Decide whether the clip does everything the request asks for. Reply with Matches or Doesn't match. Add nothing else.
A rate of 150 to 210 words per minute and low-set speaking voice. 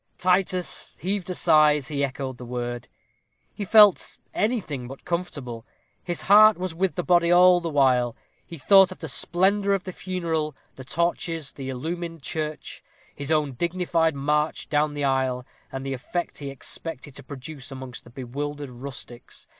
Doesn't match